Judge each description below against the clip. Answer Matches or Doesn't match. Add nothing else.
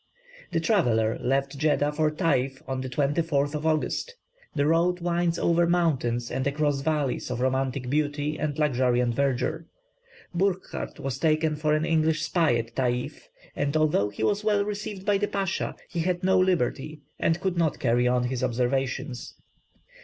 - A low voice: Doesn't match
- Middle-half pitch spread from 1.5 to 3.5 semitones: Doesn't match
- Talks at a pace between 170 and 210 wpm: Doesn't match